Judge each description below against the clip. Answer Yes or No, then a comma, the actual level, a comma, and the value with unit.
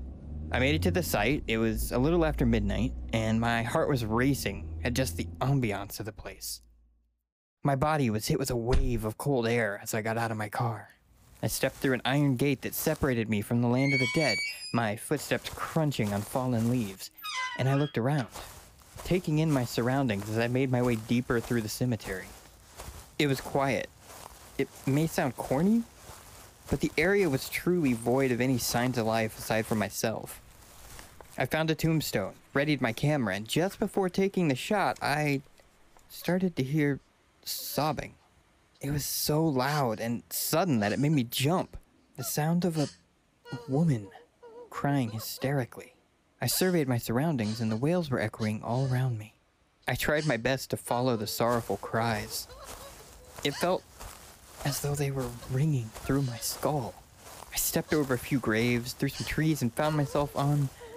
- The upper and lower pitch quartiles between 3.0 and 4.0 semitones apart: No, average, 4.5 semitones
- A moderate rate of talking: Yes, average, 175 wpm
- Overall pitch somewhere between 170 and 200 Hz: No, low, 125 Hz